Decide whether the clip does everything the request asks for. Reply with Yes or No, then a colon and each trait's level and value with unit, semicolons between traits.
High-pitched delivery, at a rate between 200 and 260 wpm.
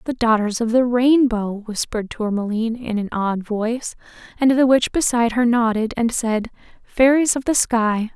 No: high, 235 Hz; average, 170 wpm